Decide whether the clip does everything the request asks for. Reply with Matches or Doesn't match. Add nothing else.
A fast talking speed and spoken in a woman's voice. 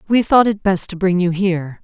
Matches